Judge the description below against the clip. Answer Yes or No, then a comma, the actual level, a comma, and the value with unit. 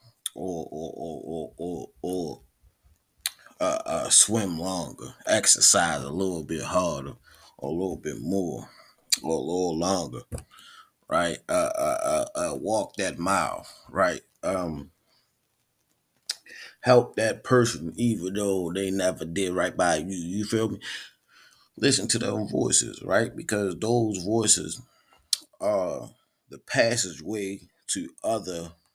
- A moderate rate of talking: No, slow, 125 wpm